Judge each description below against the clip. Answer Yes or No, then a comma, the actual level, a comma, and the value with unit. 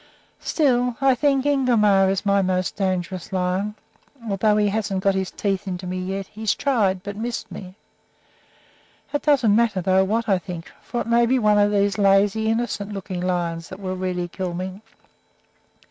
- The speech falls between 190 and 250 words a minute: No, average, 175 wpm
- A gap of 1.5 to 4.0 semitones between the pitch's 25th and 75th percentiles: Yes, average, 3.0 semitones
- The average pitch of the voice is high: Yes, high, 200 Hz